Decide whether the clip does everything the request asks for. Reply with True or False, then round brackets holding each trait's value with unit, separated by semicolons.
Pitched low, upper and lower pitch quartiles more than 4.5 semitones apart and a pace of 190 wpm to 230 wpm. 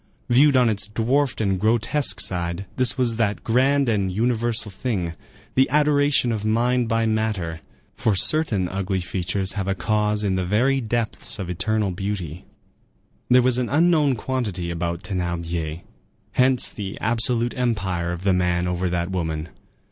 False (105 Hz; 5.1 semitones; 155 wpm)